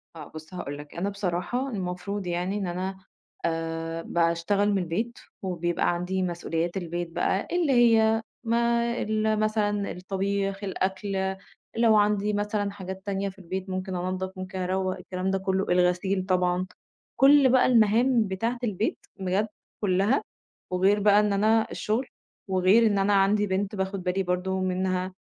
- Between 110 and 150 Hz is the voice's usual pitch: No, high, 190 Hz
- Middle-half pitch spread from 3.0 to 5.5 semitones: No, narrow, 2.4 semitones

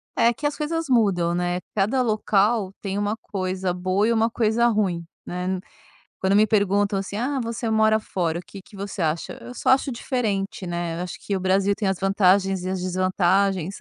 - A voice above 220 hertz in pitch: No, high, 195 Hz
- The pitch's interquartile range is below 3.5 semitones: Yes, average, 2.9 semitones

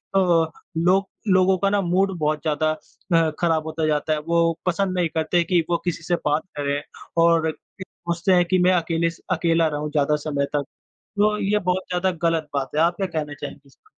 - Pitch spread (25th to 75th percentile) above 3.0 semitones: No, narrow, 2.6 semitones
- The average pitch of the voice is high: No, medium, 165 Hz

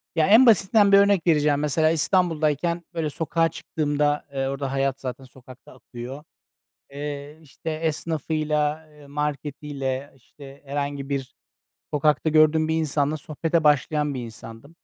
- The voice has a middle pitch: Yes, medium, 150 Hz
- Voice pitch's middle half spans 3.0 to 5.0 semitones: No, narrow, 2.5 semitones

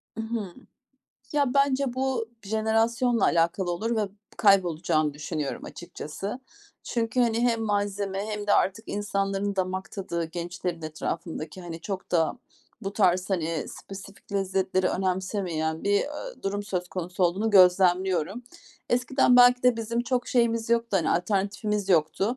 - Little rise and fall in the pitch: No, average, 4.2 semitones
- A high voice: Yes, high, 195 Hz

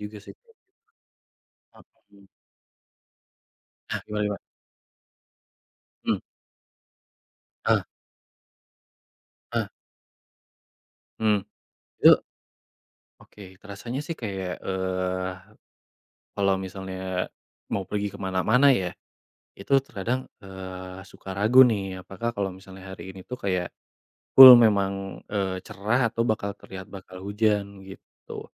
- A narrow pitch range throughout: Yes, narrow, 2.2 semitones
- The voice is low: Yes, low, 100 Hz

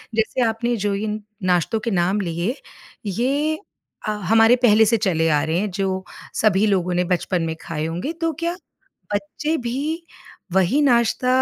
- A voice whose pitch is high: Yes, high, 210 Hz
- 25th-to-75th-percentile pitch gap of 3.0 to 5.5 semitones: Yes, average, 4.9 semitones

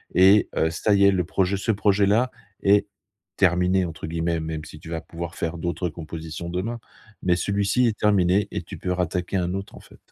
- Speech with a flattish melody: No, average, 3.0 semitones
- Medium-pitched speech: No, very low, 90 Hz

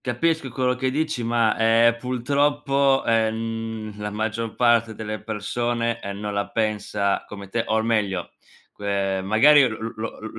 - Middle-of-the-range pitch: No, low, 115 Hz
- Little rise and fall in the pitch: Yes, narrow, 2.3 semitones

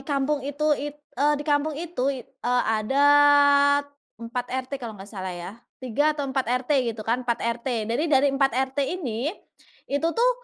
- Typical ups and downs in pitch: Yes, average, 3.2 semitones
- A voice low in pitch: No, very high, 275 Hz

